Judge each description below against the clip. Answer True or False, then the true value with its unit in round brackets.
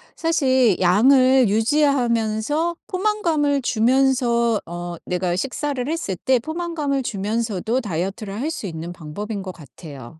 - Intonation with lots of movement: True (6.5 semitones)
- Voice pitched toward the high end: True (235 Hz)